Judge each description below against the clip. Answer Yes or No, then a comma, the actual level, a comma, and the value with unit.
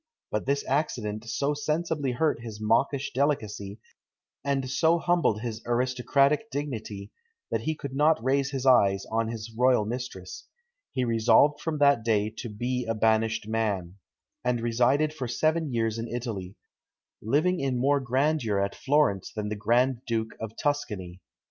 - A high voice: No, low, 120 Hz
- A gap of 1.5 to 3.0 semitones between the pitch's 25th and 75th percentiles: No, average, 4.3 semitones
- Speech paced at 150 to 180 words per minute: Yes, average, 155 wpm